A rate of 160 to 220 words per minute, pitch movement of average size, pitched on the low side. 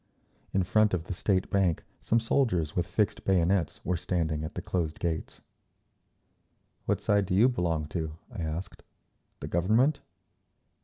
No: average, 150 wpm; average, 3.9 semitones; very low, 90 Hz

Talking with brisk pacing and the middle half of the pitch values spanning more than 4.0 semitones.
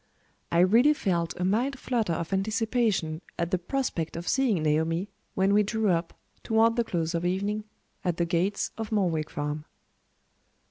No: average, 165 wpm; average, 4.8 semitones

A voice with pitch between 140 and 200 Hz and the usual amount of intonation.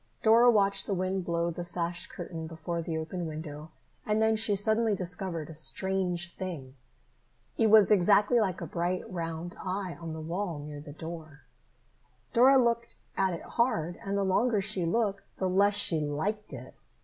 Yes: medium, 185 Hz; average, 3.8 semitones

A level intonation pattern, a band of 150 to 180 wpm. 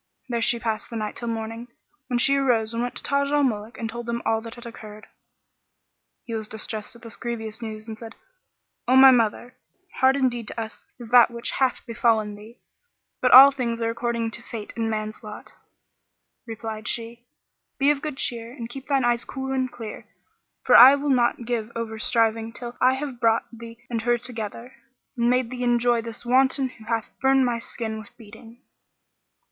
No: narrow, 1.9 semitones; average, 195 wpm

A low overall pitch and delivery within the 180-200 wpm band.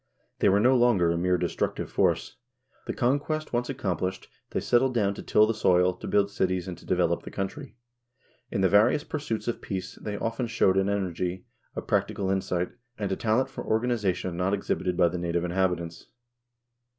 Yes: very low, 95 Hz; average, 185 wpm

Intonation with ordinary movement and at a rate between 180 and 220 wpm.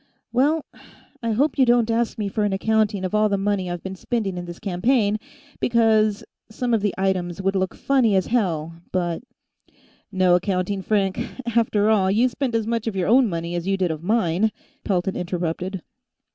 Yes: average, 3.6 semitones; average, 190 wpm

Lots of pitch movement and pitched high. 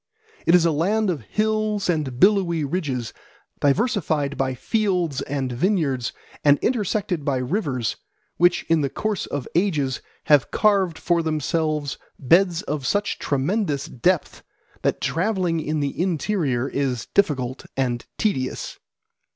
No: wide, 5.8 semitones; medium, 160 Hz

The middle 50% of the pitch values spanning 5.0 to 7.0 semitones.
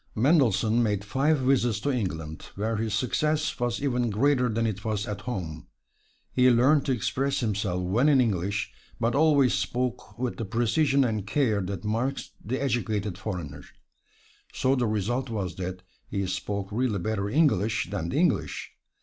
No: average, 4.3 semitones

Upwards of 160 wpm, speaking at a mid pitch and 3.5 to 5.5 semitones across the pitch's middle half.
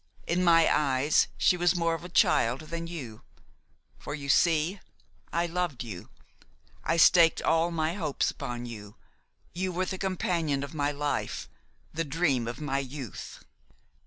No: average, 155 wpm; medium, 160 Hz; average, 3.9 semitones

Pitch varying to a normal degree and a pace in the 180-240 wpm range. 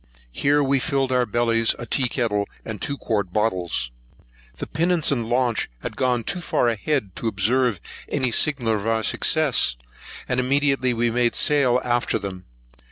No: average, 3.4 semitones; average, 165 wpm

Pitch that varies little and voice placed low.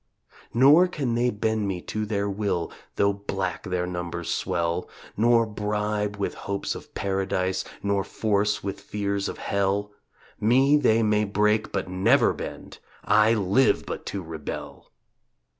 Yes: narrow, 2.1 semitones; low, 100 Hz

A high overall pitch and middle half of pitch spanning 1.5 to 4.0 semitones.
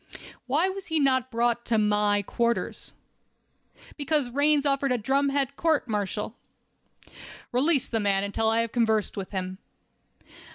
No: high, 240 Hz; average, 5.0 semitones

